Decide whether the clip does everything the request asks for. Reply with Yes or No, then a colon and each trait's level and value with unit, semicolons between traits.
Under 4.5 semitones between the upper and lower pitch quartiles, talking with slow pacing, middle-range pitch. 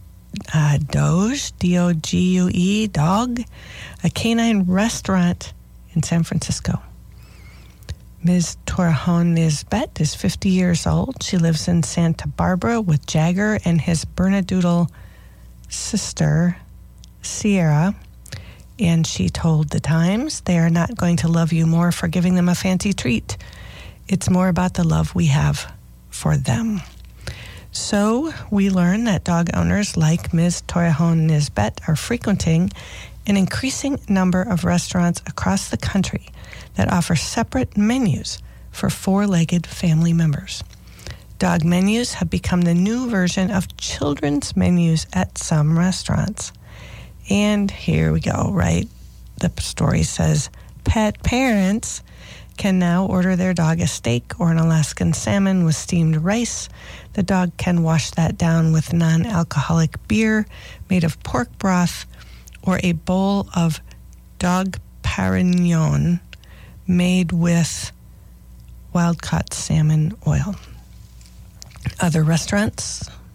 Yes: average, 3.6 semitones; slow, 125 wpm; medium, 170 Hz